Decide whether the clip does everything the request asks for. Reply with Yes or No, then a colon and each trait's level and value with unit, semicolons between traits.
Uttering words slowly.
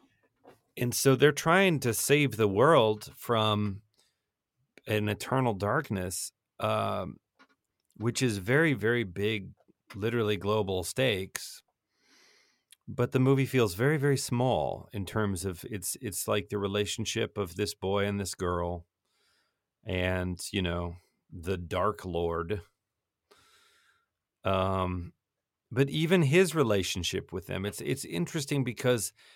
Yes: slow, 120 wpm